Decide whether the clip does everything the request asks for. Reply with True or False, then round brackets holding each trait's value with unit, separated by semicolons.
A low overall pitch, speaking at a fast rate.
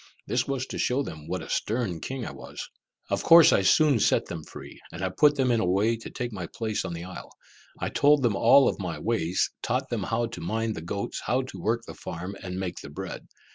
True (110 Hz; 245 wpm)